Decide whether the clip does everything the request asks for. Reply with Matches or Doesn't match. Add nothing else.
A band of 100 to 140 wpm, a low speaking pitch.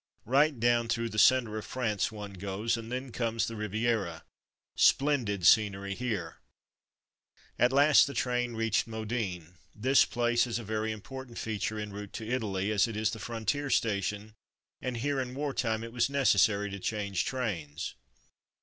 Doesn't match